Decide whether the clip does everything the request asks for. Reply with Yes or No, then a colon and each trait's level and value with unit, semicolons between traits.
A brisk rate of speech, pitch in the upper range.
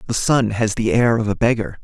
No: fast, 260 wpm; low, 110 Hz